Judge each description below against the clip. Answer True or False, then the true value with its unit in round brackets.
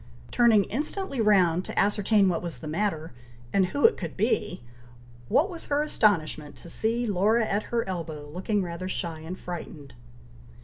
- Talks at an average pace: True (165 wpm)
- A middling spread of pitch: True (5.0 semitones)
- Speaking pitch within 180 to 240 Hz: True (190 Hz)